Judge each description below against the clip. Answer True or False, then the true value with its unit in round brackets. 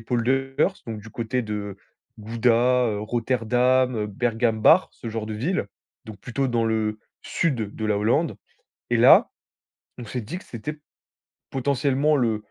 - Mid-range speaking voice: False (120 Hz)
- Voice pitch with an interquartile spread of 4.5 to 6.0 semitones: False (3.0 semitones)